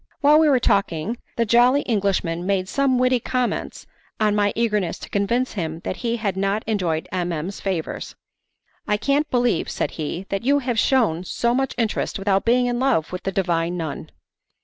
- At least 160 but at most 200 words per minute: Yes, average, 185 wpm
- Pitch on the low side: No, high, 210 Hz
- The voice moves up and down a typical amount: Yes, average, 5.0 semitones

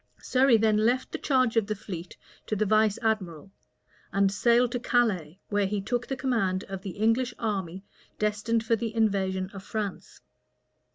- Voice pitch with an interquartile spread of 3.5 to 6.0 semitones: No, average, 3.0 semitones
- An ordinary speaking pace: Yes, average, 170 wpm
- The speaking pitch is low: No, high, 215 Hz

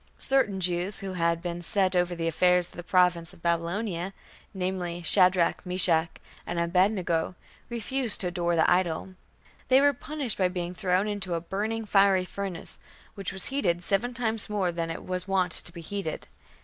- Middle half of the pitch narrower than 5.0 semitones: Yes, narrow, 2.5 semitones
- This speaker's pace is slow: No, average, 175 wpm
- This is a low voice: No, medium, 180 Hz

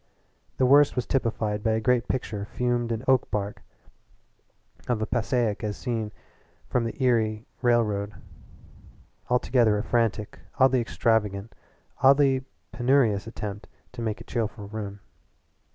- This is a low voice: Yes, low, 115 Hz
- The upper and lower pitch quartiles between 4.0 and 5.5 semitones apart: No, average, 2.8 semitones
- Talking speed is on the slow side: Yes, slow, 125 wpm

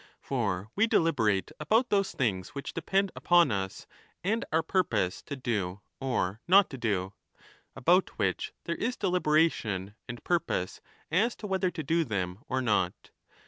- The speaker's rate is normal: Yes, average, 155 wpm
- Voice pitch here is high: No, medium, 140 Hz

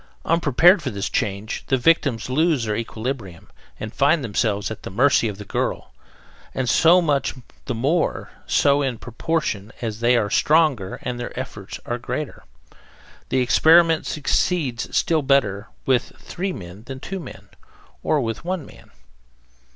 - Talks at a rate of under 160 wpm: Yes, average, 150 wpm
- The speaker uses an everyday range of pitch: No, wide, 5.8 semitones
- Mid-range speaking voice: No, low, 130 Hz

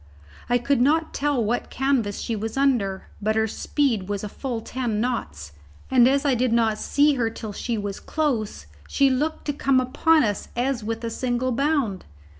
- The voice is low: No, high, 245 Hz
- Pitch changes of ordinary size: Yes, average, 3.9 semitones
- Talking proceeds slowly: No, average, 190 wpm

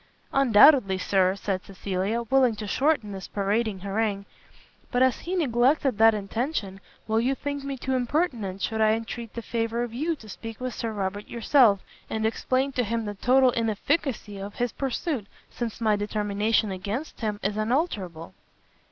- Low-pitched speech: No, high, 225 Hz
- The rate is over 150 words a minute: Yes, average, 165 wpm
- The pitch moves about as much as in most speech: Yes, average, 3.9 semitones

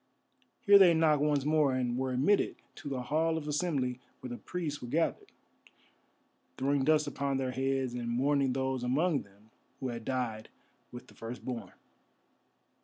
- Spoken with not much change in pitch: No, average, 3.2 semitones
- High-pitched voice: No, low, 135 Hz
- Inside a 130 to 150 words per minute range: No, average, 160 wpm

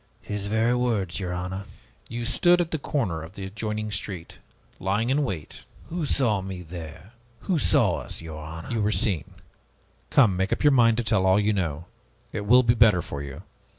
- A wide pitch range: No, average, 4.7 semitones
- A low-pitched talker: Yes, low, 100 Hz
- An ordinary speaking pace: Yes, average, 195 wpm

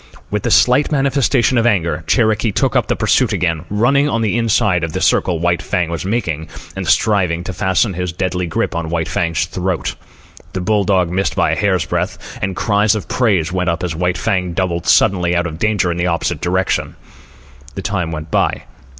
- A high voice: No, very low, 90 Hz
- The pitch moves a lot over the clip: No, average, 3.7 semitones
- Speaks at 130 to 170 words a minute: No, average, 200 wpm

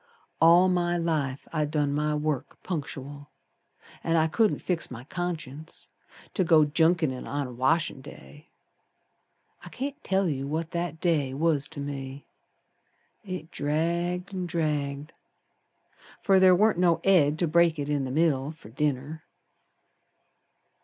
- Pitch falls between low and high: Yes, medium, 155 Hz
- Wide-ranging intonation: No, average, 3.2 semitones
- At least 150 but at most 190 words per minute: No, average, 140 wpm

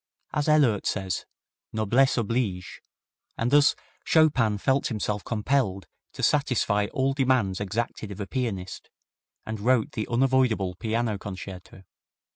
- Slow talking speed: Yes, slow, 120 wpm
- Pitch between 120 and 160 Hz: No, low, 110 Hz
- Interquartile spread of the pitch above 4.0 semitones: Yes, average, 4.5 semitones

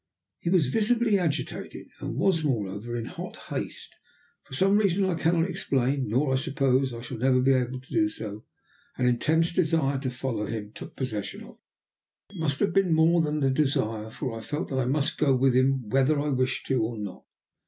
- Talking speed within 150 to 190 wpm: No, fast, 205 wpm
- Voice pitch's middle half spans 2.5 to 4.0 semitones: No, average, 4.4 semitones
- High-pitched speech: No, low, 135 Hz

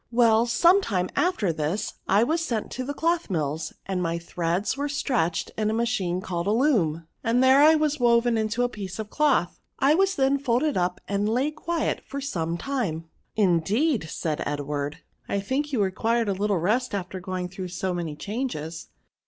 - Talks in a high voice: Yes, high, 215 Hz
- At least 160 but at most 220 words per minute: Yes, average, 195 wpm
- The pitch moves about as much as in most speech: No, wide, 7.0 semitones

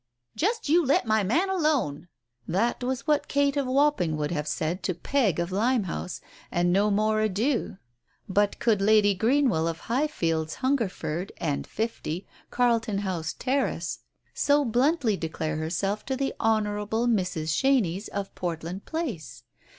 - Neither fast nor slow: Yes, average, 150 wpm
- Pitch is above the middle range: Yes, high, 210 Hz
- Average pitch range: No, wide, 7.1 semitones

